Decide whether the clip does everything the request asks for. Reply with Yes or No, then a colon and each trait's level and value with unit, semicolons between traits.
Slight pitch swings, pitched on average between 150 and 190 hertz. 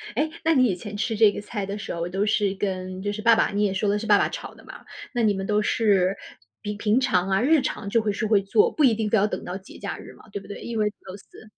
No: narrow, 2.2 semitones; high, 205 Hz